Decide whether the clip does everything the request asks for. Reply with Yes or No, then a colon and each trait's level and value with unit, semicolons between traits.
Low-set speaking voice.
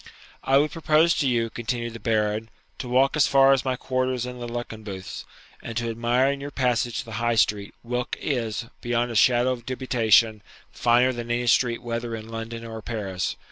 Yes: low, 120 Hz